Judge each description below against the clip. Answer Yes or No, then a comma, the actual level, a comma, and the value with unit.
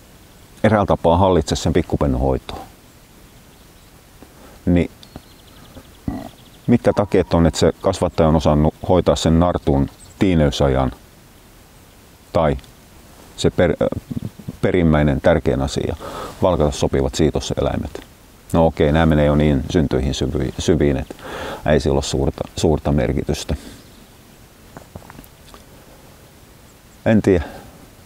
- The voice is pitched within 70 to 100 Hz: Yes, very low, 80 Hz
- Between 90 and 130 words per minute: Yes, average, 100 wpm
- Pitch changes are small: No, average, 3.6 semitones